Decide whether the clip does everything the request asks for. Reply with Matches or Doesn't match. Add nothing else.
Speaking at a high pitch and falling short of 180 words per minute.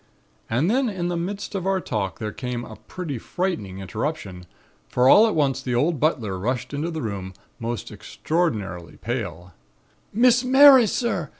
Doesn't match